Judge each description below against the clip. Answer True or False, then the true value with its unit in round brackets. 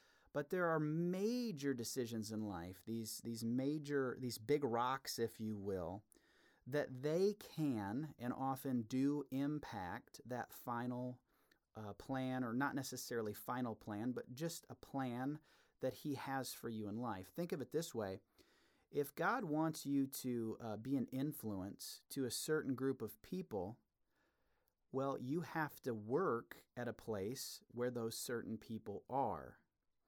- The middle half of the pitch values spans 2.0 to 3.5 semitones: False (4.3 semitones)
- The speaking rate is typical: True (150 wpm)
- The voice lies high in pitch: False (130 Hz)